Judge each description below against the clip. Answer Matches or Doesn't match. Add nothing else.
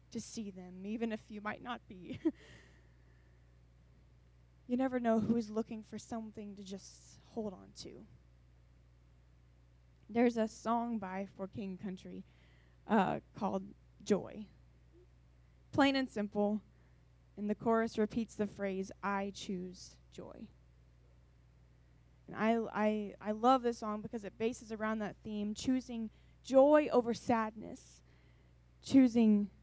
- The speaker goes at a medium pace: Doesn't match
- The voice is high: Matches